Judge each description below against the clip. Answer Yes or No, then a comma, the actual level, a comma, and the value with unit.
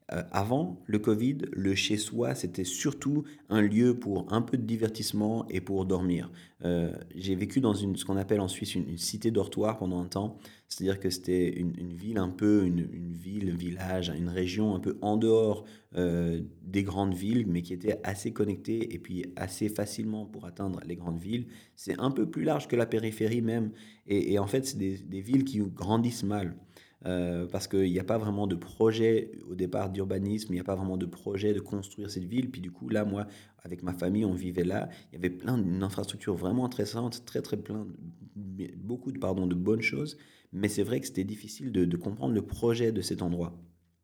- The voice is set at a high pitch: No, low, 100 Hz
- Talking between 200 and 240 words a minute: Yes, average, 215 wpm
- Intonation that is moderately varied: Yes, average, 3.2 semitones